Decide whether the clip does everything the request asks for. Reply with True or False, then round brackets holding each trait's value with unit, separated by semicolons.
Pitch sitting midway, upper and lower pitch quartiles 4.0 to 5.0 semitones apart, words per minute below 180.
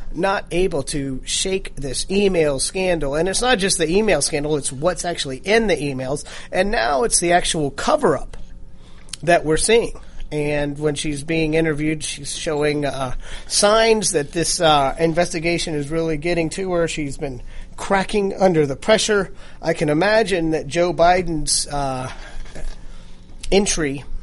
True (160 Hz; 4.4 semitones; 155 wpm)